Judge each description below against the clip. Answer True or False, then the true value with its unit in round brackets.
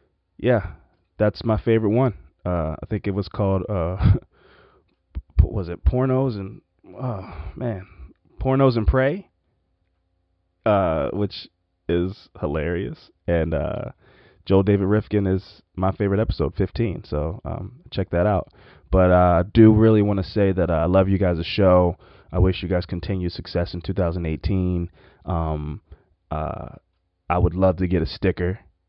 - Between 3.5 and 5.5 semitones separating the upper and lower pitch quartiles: False (3.0 semitones)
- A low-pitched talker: True (95 Hz)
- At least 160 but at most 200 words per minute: False (150 wpm)